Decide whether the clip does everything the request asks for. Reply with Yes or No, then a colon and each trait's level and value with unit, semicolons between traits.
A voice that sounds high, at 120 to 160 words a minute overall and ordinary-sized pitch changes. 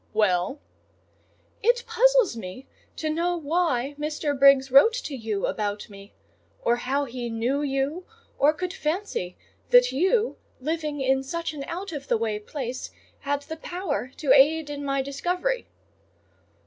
Yes: very high, 285 Hz; average, 150 wpm; average, 4.8 semitones